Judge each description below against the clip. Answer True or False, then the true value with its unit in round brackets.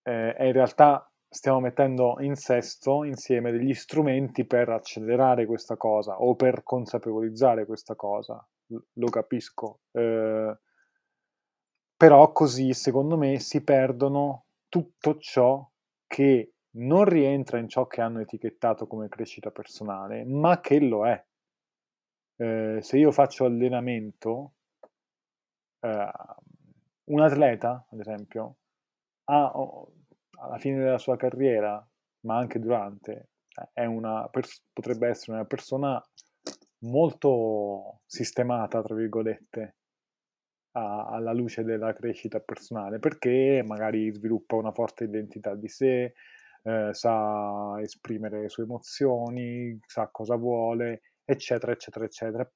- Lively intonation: False (3.2 semitones)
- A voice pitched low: True (120 Hz)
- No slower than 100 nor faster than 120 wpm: True (115 wpm)